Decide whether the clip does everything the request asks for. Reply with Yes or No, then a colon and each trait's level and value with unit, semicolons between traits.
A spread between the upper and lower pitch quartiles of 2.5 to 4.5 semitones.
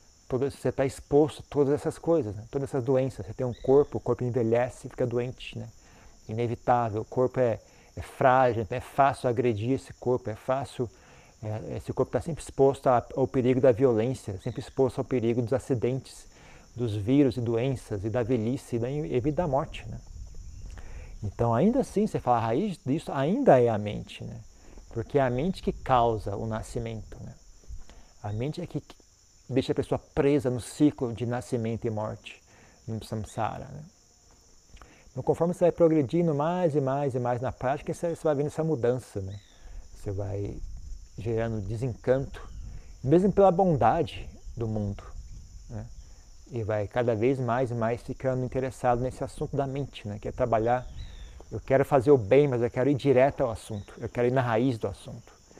Yes: average, 4.2 semitones